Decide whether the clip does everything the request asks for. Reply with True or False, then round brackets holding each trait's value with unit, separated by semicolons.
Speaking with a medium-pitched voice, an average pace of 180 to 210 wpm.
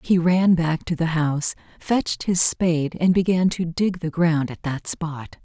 True (165 Hz; 200 wpm)